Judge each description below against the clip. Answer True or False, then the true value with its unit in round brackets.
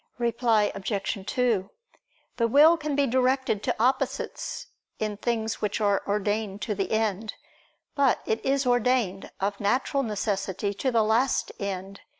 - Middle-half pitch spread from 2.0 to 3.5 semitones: False (3.9 semitones)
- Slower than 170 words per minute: True (145 wpm)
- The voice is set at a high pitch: True (220 Hz)